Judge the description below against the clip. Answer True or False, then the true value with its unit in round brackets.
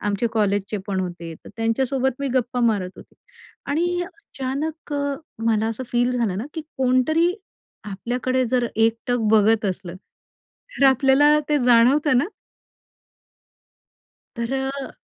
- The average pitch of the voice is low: False (245 Hz)